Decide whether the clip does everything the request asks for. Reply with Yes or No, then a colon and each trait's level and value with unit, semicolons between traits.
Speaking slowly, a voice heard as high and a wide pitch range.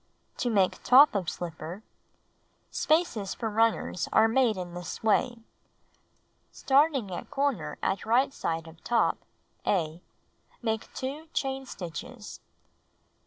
Yes: slow, 120 wpm; high, 220 Hz; wide, 6.6 semitones